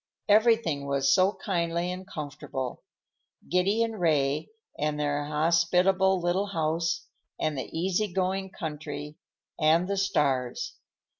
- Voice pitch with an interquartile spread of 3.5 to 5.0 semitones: Yes, average, 4.3 semitones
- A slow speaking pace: Yes, slow, 120 wpm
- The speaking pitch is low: No, medium, 170 Hz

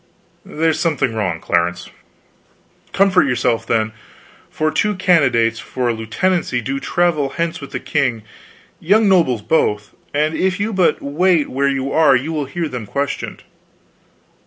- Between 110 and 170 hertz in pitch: Yes, medium, 140 Hz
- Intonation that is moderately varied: No, wide, 6.3 semitones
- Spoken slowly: No, average, 145 wpm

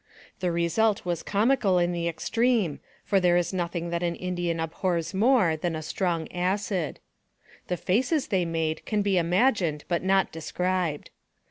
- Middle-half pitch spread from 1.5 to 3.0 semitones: Yes, average, 2.7 semitones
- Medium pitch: Yes, medium, 180 Hz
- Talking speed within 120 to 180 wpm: Yes, average, 155 wpm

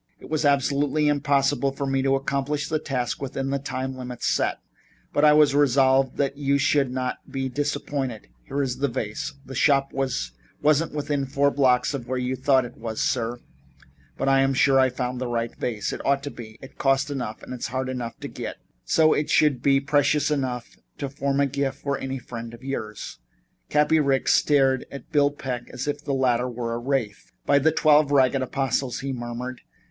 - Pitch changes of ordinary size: No, narrow, 2.1 semitones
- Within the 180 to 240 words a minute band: Yes, average, 195 wpm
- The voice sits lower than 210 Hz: Yes, low, 135 Hz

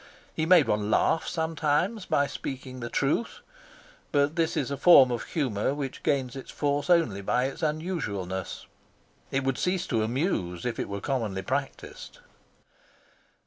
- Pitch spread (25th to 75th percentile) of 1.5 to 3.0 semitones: No, average, 5.3 semitones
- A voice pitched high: No, low, 135 Hz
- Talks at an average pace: Yes, average, 150 wpm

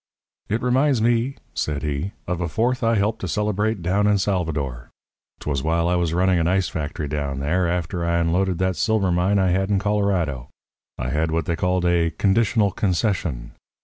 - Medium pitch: No, very low, 90 Hz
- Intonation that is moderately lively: Yes, average, 4.1 semitones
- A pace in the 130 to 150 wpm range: No, average, 185 wpm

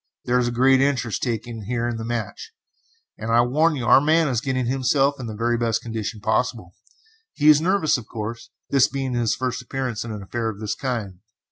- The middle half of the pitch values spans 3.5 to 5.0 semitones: No, average, 2.9 semitones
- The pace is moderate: No, fast, 215 wpm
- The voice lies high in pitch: No, low, 120 Hz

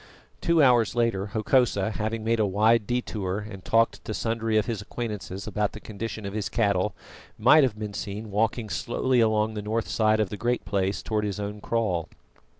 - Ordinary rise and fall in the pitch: No, narrow, 2.0 semitones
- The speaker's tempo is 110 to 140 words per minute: No, average, 190 wpm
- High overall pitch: No, low, 110 Hz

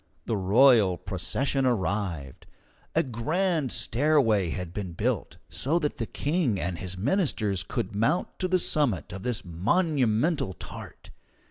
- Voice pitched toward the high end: No, low, 115 Hz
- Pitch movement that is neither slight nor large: No, wide, 7.6 semitones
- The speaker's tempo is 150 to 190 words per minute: No, slow, 135 wpm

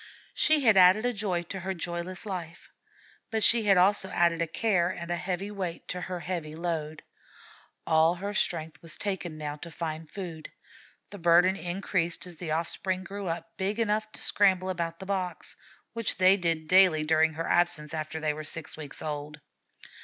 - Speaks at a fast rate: No, average, 185 wpm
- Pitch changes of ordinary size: Yes, average, 3.0 semitones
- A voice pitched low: No, medium, 175 Hz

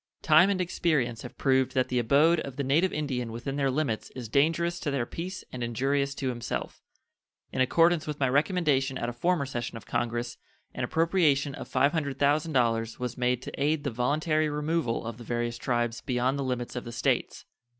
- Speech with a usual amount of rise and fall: Yes, average, 4.1 semitones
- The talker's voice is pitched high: No, low, 135 Hz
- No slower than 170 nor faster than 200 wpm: Yes, average, 190 wpm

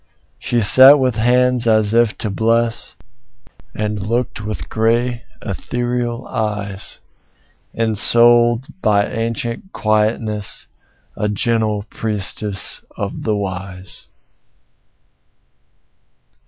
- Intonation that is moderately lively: No, narrow, 2.2 semitones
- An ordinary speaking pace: No, slow, 85 wpm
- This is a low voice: Yes, low, 110 Hz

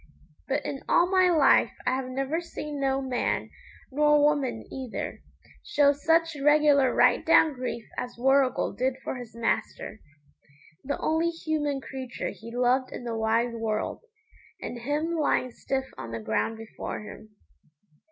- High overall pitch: Yes, very high, 265 Hz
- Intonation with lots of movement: No, average, 3.7 semitones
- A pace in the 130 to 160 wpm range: Yes, average, 150 wpm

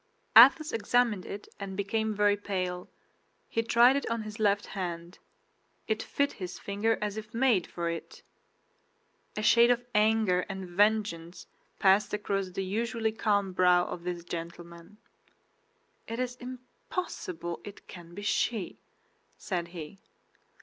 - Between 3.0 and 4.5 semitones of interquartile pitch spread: Yes, average, 3.8 semitones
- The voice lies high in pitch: Yes, high, 205 Hz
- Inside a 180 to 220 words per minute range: No, slow, 135 wpm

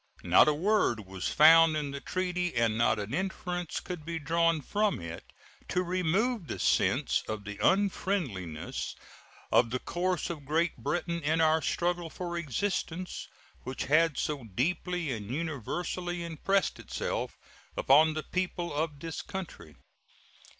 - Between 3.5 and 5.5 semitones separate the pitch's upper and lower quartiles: Yes, average, 4.2 semitones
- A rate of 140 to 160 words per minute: Yes, average, 145 wpm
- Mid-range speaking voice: Yes, medium, 165 Hz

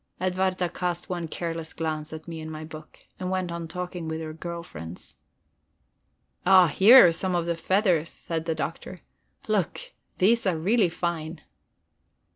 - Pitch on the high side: No, medium, 170 Hz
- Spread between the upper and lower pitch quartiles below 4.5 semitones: Yes, narrow, 2.4 semitones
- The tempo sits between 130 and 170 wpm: Yes, average, 160 wpm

